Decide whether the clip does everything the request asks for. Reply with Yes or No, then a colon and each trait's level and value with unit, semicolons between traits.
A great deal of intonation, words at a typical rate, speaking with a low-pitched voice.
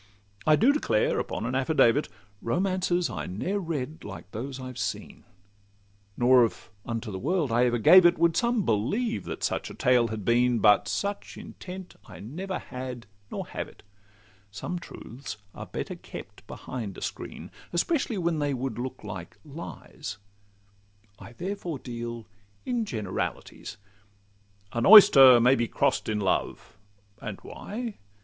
Yes: wide, 7.5 semitones; average, 150 wpm; low, 130 Hz